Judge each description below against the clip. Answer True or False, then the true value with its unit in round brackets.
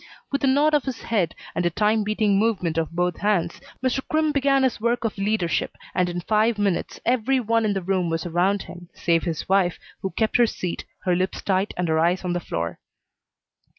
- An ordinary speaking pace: False (215 wpm)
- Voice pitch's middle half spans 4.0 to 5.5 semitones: True (4.7 semitones)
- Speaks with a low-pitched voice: False (195 Hz)